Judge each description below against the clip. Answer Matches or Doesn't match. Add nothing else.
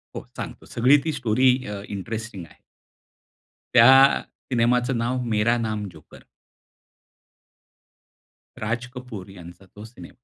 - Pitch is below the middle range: Matches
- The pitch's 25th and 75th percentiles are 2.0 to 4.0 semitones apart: Matches